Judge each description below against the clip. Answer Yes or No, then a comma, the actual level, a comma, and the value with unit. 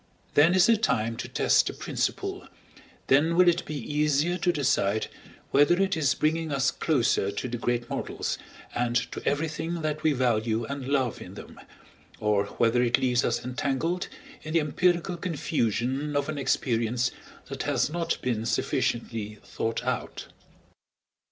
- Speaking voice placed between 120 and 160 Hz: Yes, medium, 140 Hz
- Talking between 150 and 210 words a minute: Yes, average, 155 wpm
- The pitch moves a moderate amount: Yes, average, 5.0 semitones